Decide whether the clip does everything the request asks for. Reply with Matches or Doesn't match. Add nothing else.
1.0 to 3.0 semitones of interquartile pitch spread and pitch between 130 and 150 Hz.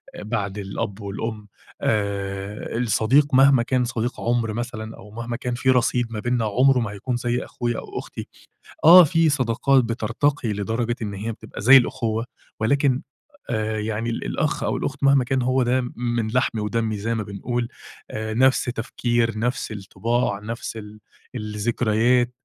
Doesn't match